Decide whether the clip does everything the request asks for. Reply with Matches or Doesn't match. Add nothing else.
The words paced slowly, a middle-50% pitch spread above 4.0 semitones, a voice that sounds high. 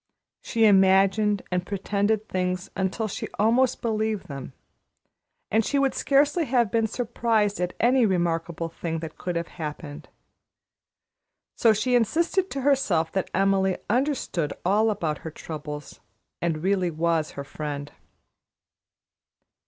Matches